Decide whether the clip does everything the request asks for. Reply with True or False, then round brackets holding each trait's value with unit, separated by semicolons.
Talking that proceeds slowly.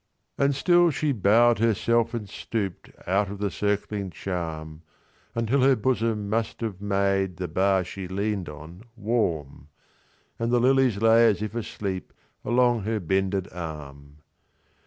True (120 wpm)